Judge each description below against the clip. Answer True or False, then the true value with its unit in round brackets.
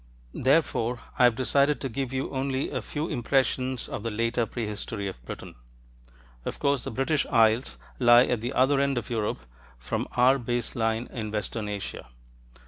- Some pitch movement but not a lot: True (3.0 semitones)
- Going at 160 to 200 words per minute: True (170 wpm)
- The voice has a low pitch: True (120 Hz)